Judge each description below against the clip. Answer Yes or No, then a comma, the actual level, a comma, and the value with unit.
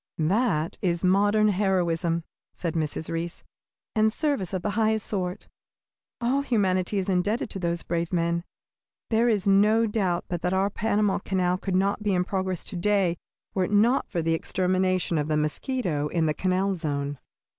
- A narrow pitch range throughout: No, average, 3.3 semitones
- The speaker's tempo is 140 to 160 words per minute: No, average, 170 wpm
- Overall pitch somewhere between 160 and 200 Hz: Yes, medium, 185 Hz